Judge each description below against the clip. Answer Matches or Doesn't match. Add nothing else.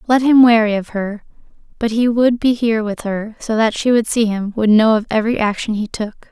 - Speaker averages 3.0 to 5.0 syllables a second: Doesn't match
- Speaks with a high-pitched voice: Matches